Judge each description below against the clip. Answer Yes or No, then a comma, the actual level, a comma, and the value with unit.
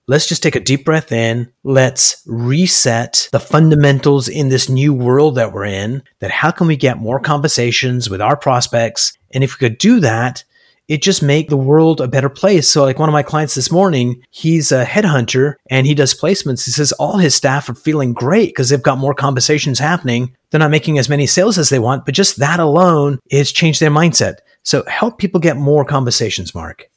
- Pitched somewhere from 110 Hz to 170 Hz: Yes, medium, 140 Hz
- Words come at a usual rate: No, fast, 210 wpm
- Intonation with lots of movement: No, average, 3.4 semitones